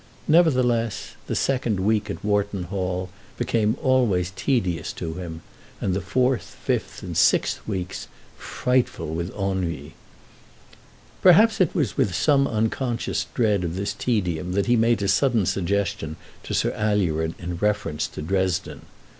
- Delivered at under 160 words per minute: Yes, average, 140 wpm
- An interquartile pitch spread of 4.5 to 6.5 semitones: Yes, average, 4.8 semitones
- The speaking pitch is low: Yes, low, 100 Hz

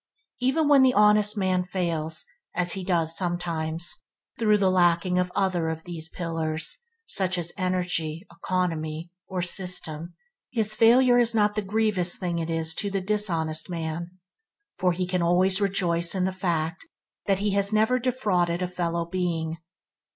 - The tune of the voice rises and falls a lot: No, average, 3.1 semitones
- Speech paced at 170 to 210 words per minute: No, average, 155 wpm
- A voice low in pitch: No, medium, 180 Hz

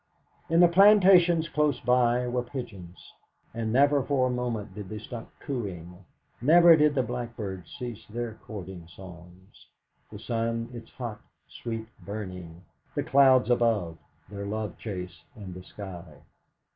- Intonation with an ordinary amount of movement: Yes, average, 5.0 semitones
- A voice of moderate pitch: No, low, 115 Hz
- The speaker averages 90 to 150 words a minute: Yes, average, 140 wpm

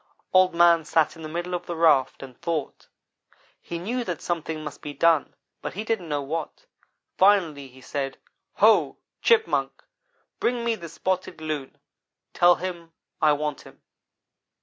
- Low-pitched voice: No, medium, 165 Hz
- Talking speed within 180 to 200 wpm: No, average, 155 wpm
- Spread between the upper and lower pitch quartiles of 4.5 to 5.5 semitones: No, average, 3.2 semitones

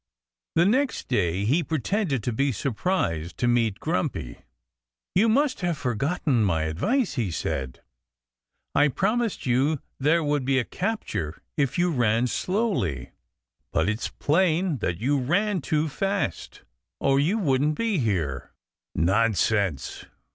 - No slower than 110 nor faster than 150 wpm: Yes, slow, 135 wpm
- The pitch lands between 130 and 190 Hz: Yes, low, 135 Hz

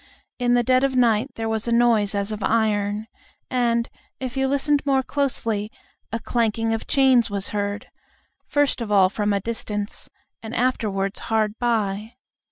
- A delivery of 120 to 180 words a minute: Yes, average, 165 wpm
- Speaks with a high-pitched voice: Yes, high, 225 Hz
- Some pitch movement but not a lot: Yes, average, 3.1 semitones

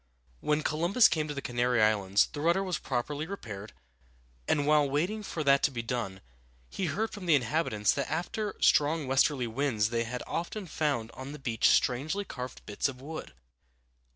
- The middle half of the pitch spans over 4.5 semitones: Yes, average, 4.9 semitones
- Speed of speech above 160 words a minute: Yes, average, 180 wpm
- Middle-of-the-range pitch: Yes, medium, 145 Hz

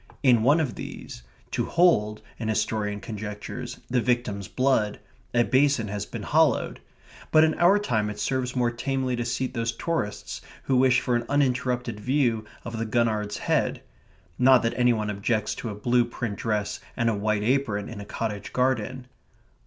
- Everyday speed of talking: Yes, average, 175 wpm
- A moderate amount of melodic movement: Yes, average, 3.4 semitones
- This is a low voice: Yes, low, 120 Hz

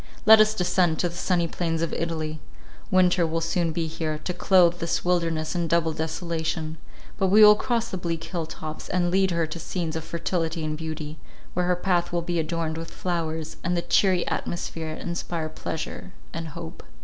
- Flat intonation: Yes, narrow, 1.8 semitones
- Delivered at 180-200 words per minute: Yes, average, 190 wpm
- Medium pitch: Yes, medium, 170 Hz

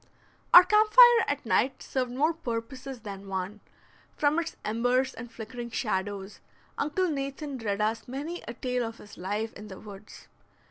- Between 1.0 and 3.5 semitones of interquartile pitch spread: No, average, 5.2 semitones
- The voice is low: No, high, 245 Hz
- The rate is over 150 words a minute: Yes, average, 160 wpm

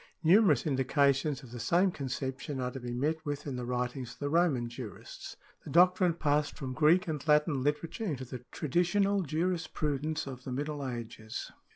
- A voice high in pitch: No, medium, 145 Hz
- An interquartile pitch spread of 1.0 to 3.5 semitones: No, average, 4.0 semitones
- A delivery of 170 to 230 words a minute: Yes, average, 175 wpm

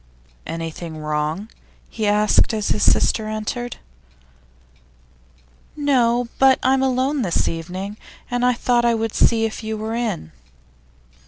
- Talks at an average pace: No, slow, 130 wpm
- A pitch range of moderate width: Yes, average, 4.0 semitones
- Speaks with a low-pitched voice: No, high, 220 Hz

